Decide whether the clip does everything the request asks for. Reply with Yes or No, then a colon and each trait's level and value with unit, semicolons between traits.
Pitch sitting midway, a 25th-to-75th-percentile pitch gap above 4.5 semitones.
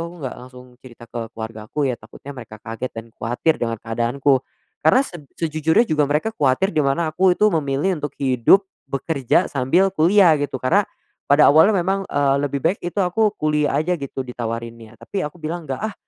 Yes: medium, 145 Hz; average, 5.3 semitones